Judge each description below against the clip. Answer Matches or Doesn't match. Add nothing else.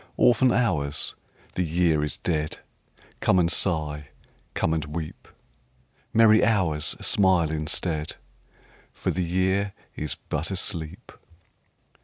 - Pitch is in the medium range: Doesn't match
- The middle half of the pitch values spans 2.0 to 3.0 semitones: Doesn't match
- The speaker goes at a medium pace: Doesn't match